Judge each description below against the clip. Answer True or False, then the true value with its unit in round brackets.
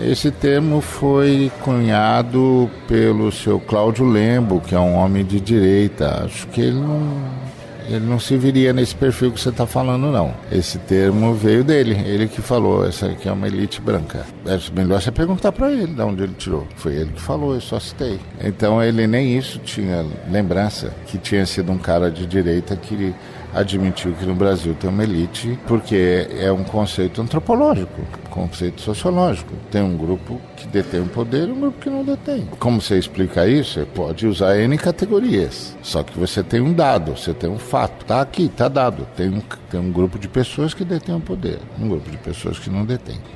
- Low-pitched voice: True (110 Hz)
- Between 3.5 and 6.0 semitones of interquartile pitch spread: True (5.3 semitones)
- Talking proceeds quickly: True (195 wpm)